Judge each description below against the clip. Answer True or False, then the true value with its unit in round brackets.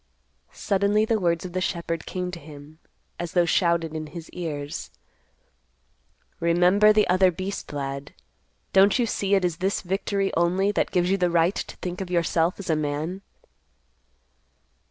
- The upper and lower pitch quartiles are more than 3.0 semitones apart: False (2.7 semitones)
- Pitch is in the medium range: True (180 Hz)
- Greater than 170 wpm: False (160 wpm)